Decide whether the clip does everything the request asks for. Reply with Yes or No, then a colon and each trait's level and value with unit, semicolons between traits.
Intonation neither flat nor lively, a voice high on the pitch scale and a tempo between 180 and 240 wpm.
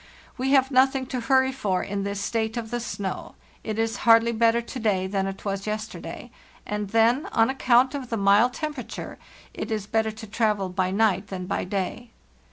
Yes: average, 3.4 semitones; high, 220 Hz; average, 190 wpm